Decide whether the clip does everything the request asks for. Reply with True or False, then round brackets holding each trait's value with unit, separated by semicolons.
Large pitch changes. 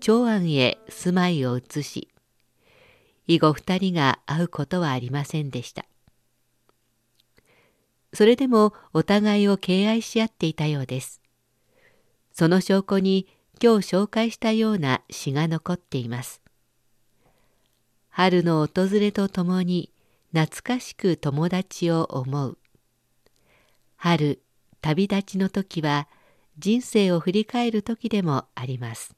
True (7.0 semitones)